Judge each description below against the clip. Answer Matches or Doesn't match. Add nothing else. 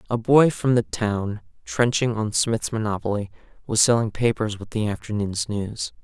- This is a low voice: Matches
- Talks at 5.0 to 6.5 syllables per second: Doesn't match